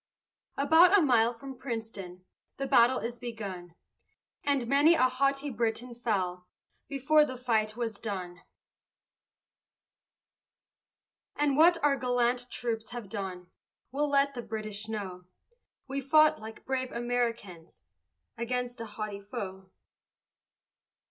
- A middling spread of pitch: Yes, average, 4.2 semitones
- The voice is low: No, high, 240 Hz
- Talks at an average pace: No, slow, 115 wpm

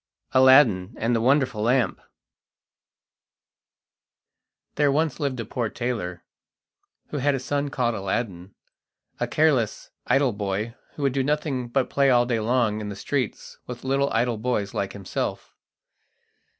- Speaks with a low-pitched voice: Yes, low, 125 Hz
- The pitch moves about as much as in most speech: Yes, average, 4.2 semitones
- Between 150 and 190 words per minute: No, average, 140 wpm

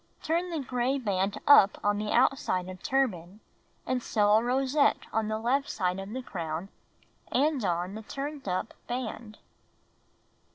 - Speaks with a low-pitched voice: No, high, 220 Hz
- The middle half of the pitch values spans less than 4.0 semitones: No, wide, 5.5 semitones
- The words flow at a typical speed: Yes, average, 155 wpm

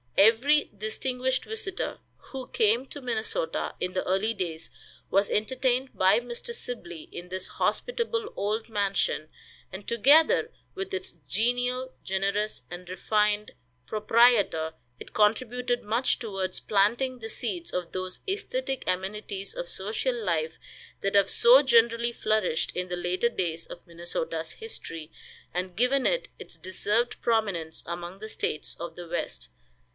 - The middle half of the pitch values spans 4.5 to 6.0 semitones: Yes, average, 5.2 semitones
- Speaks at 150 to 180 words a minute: No, slow, 135 wpm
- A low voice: No, high, 215 Hz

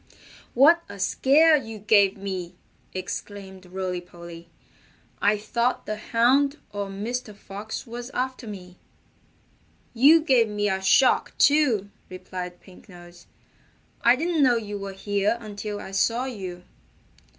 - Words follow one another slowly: Yes, slow, 130 wpm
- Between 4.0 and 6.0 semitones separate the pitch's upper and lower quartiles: Yes, average, 4.3 semitones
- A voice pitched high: Yes, high, 205 Hz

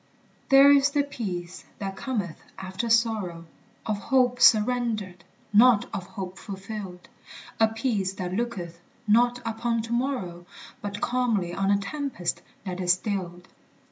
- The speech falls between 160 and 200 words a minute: No, slow, 135 wpm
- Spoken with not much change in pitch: No, average, 4.3 semitones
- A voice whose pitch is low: No, high, 205 Hz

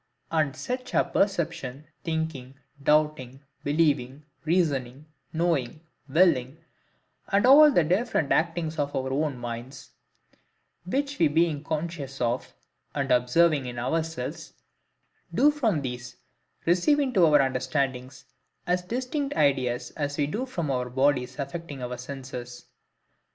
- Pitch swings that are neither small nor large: Yes, average, 4.6 semitones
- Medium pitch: Yes, medium, 150 Hz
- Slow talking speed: Yes, slow, 115 wpm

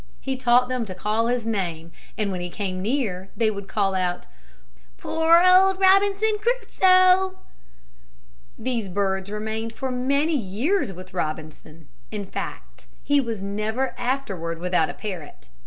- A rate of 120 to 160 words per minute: Yes, average, 140 wpm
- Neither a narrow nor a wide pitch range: No, wide, 6.9 semitones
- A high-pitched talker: Yes, high, 220 Hz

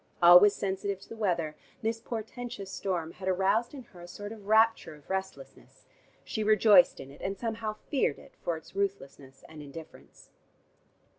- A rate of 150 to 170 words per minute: Yes, average, 165 wpm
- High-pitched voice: Yes, high, 195 Hz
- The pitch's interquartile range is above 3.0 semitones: Yes, average, 4.1 semitones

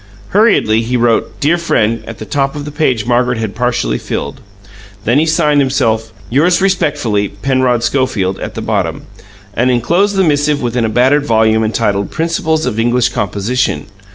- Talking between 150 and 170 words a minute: Yes, average, 165 wpm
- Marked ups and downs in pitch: No, average, 4.7 semitones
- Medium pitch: No, low, 125 Hz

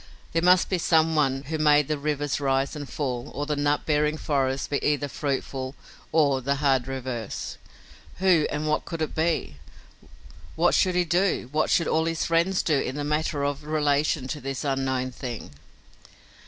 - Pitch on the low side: No, medium, 145 Hz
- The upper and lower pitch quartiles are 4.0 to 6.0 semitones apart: No, average, 2.8 semitones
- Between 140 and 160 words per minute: No, average, 180 wpm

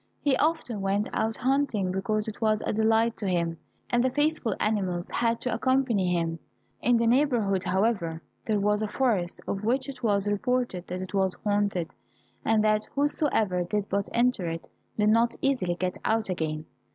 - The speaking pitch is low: No, high, 215 Hz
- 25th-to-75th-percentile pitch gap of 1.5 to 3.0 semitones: No, average, 4.2 semitones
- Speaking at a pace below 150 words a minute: No, average, 175 wpm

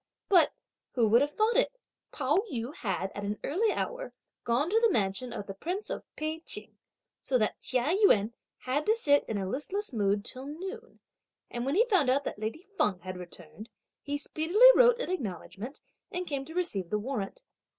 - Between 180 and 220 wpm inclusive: Yes, average, 190 wpm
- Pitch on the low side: No, very high, 275 Hz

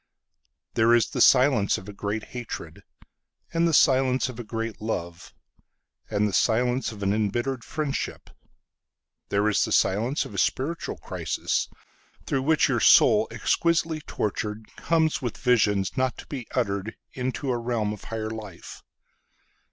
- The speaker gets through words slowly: Yes, slow, 130 wpm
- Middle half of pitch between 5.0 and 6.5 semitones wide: No, average, 3.9 semitones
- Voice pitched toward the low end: Yes, low, 115 Hz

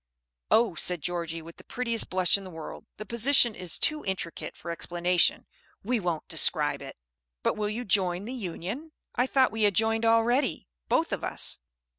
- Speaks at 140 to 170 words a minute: No, average, 180 wpm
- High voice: Yes, high, 205 Hz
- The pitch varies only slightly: No, average, 5.0 semitones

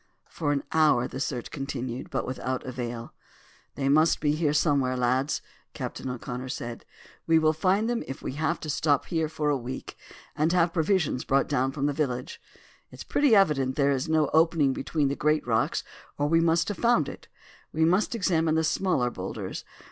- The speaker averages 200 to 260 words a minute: No, average, 185 wpm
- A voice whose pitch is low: No, medium, 145 Hz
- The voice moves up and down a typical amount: Yes, average, 3.7 semitones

